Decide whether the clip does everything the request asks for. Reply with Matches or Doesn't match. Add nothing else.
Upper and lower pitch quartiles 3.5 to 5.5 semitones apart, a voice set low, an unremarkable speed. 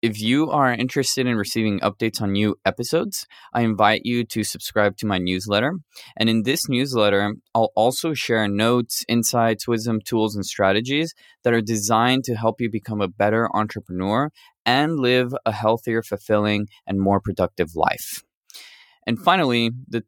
Doesn't match